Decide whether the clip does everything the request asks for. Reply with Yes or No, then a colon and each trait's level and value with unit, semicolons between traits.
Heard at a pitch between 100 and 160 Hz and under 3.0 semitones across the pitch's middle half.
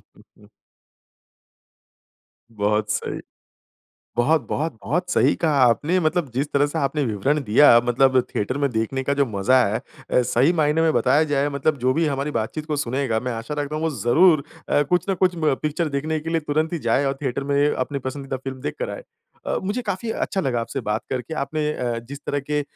No: medium, 140 Hz; average, 3.7 semitones